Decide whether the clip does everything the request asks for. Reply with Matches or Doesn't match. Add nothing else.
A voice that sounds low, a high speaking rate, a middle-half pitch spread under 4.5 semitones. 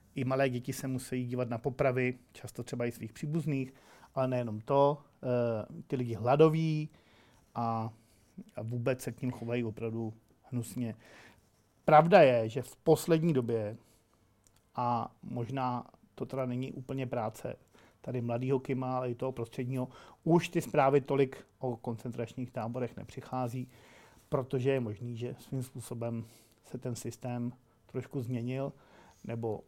Doesn't match